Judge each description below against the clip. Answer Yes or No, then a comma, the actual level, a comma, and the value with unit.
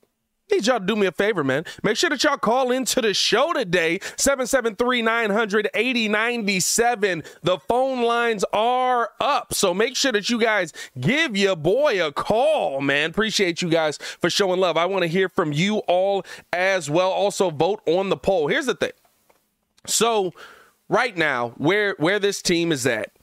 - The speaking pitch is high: Yes, high, 205 Hz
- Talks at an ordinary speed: Yes, average, 180 wpm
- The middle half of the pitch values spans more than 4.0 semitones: Yes, average, 4.6 semitones